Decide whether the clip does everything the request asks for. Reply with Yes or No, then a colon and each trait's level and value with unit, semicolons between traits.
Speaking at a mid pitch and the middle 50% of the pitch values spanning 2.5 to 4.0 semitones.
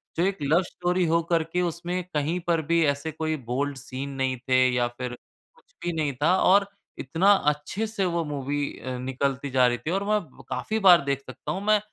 No: medium, 160 Hz; average, 5.0 semitones